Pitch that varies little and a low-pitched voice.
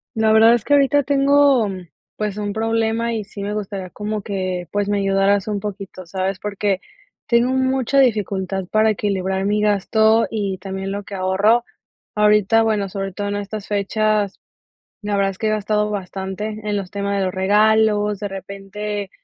No: narrow, 1.9 semitones; high, 205 Hz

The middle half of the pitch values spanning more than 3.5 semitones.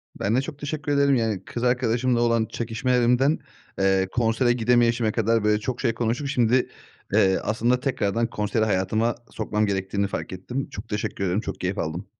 No: average, 3.0 semitones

